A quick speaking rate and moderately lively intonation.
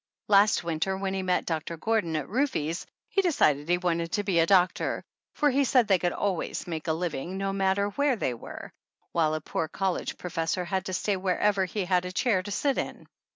Yes: fast, 210 wpm; average, 3.2 semitones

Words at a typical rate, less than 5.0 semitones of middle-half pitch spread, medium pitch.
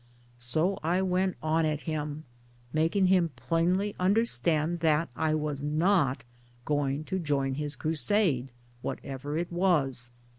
Yes: average, 145 wpm; average, 3.6 semitones; medium, 155 Hz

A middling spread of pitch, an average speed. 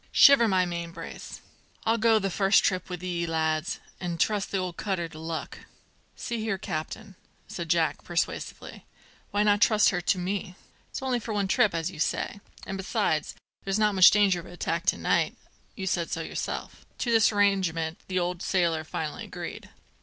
Yes: average, 3.2 semitones; average, 185 wpm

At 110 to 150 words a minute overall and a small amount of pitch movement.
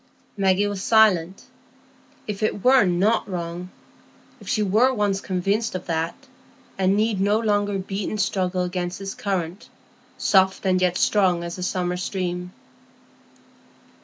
Yes: slow, 135 wpm; narrow, 2.3 semitones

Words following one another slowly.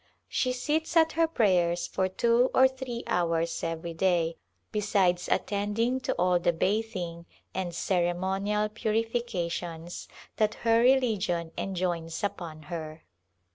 Yes: slow, 120 wpm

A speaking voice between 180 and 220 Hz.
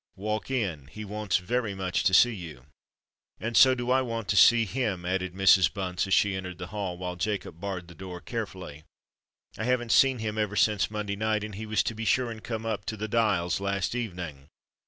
No: low, 105 Hz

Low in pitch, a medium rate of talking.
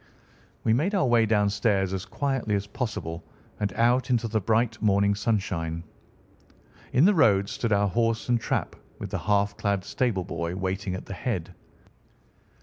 Yes: low, 105 Hz; average, 160 wpm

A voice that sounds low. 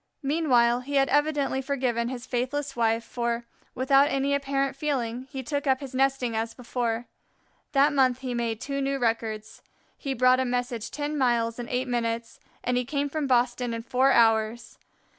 No: very high, 255 Hz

